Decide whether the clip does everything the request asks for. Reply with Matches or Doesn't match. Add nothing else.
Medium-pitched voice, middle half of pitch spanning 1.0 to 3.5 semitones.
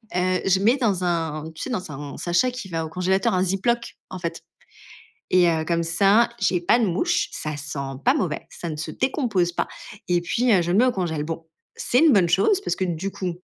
Doesn't match